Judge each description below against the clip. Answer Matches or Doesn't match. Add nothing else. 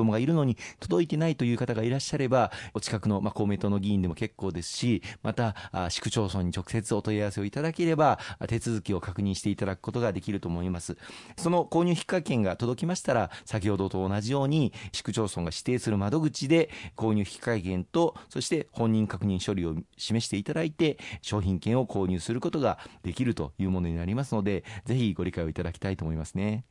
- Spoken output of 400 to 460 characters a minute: Matches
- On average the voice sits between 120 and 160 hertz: Doesn't match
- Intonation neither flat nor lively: Matches